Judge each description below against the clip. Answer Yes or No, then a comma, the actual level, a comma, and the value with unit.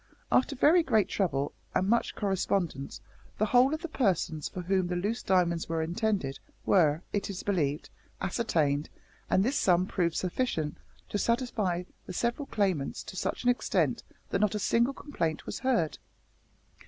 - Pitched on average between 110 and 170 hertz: No, high, 190 Hz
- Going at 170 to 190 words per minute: No, average, 160 wpm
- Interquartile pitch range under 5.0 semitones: No, wide, 5.6 semitones